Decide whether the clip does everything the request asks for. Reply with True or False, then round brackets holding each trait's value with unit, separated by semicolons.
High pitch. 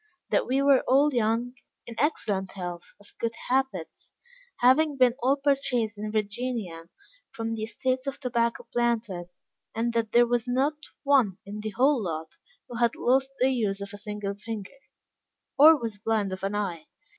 True (230 Hz)